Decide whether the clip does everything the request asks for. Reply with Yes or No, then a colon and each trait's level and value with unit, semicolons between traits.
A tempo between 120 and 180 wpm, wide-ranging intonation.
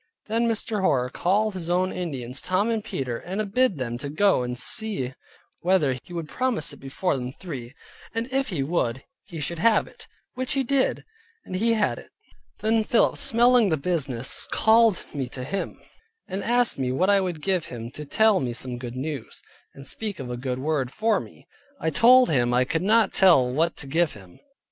No: average, 195 wpm; wide, 8.5 semitones